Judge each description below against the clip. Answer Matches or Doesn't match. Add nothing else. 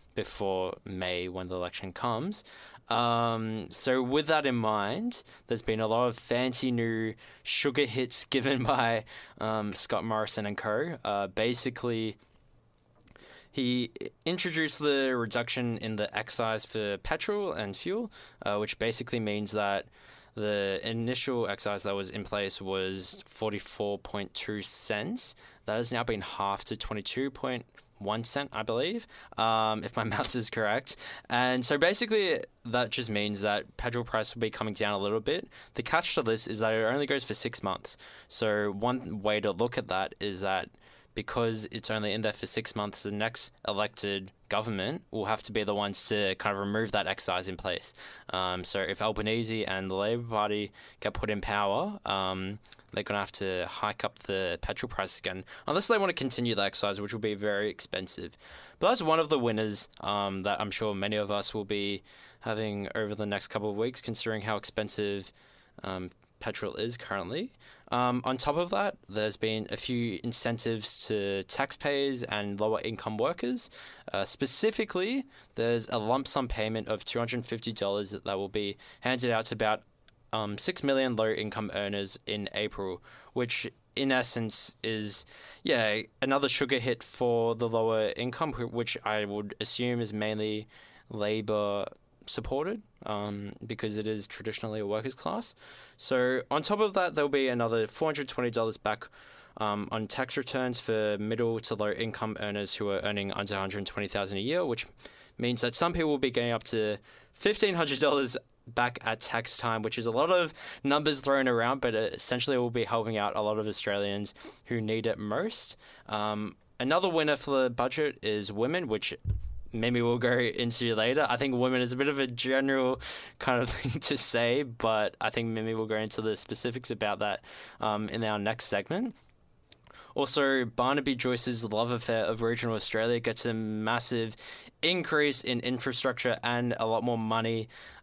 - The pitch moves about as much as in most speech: Matches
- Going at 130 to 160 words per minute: Doesn't match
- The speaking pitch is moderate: Doesn't match